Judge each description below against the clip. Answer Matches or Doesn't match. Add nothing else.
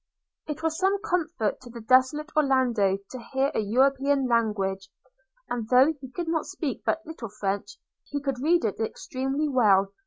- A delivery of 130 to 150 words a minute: Doesn't match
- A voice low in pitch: Doesn't match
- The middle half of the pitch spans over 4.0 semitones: Matches